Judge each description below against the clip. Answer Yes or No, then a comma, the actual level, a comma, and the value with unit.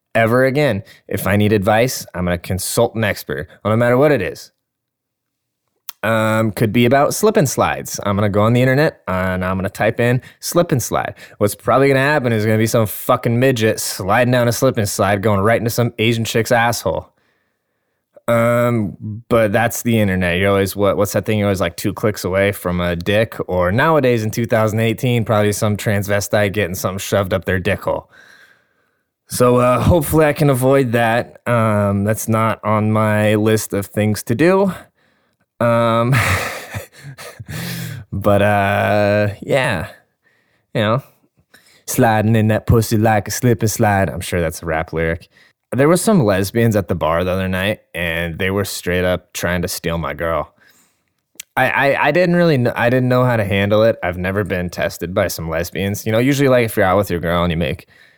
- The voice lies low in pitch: Yes, low, 110 Hz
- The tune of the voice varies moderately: Yes, average, 3.3 semitones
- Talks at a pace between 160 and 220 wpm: Yes, average, 190 wpm